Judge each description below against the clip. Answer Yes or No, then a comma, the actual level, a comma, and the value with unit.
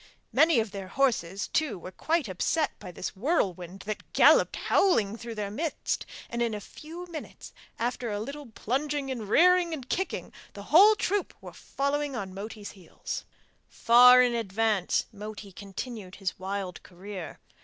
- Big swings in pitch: Yes, wide, 6.6 semitones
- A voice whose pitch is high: Yes, high, 225 Hz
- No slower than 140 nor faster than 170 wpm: Yes, average, 155 wpm